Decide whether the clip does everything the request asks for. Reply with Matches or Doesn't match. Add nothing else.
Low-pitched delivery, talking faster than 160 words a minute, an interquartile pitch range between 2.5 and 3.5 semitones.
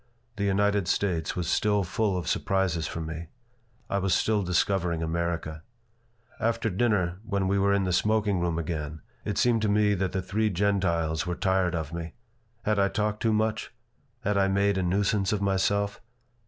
Matches